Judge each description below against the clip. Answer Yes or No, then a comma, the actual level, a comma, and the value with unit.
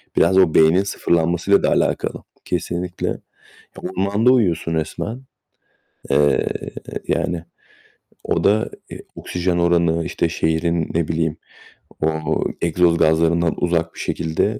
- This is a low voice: Yes, very low, 85 Hz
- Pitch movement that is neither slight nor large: No, narrow, 1.7 semitones